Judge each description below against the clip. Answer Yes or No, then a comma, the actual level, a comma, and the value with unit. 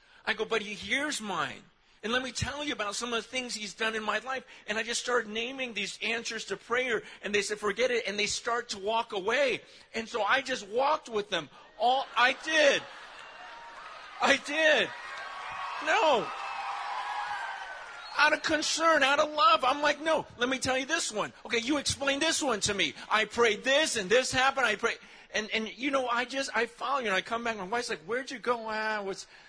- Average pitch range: Yes, average, 4.2 semitones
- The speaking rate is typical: No, fast, 215 wpm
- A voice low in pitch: No, high, 240 Hz